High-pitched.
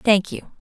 Yes: high, 205 Hz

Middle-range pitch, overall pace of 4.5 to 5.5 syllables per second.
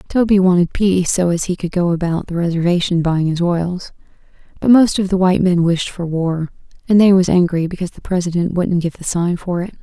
No: medium, 180 Hz; 5.7 syllables/s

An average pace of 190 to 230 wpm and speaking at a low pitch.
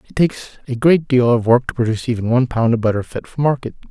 No: fast, 260 wpm; low, 125 Hz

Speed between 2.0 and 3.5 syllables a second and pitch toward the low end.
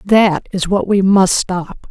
No: 3.4 syllables/s; high, 190 Hz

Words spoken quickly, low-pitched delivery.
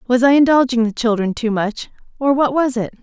No: fast, 220 wpm; high, 245 Hz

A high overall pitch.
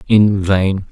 No: low, 100 Hz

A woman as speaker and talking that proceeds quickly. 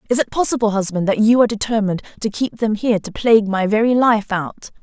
Yes: female; fast, 225 wpm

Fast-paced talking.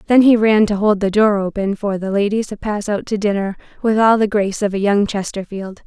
Yes: fast, 245 wpm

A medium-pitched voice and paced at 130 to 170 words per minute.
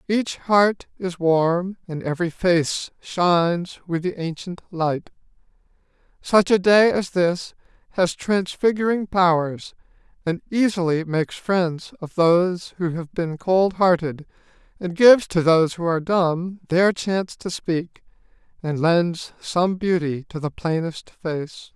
Yes: medium, 175 Hz; average, 140 wpm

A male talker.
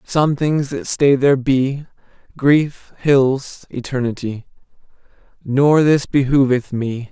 Yes: male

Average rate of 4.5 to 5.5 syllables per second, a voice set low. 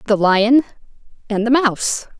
No: 4.7 syllables/s; high, 230 Hz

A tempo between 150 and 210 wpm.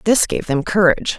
Yes: average, 200 wpm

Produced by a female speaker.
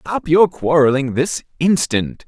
No: male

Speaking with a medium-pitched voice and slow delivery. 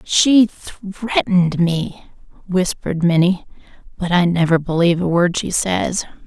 Yes: medium, 180 Hz; slow, 125 wpm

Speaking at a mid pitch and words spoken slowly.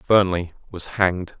No: very low, 90 Hz; slow, 130 wpm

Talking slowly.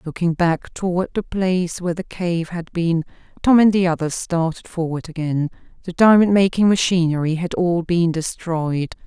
No: average, 165 wpm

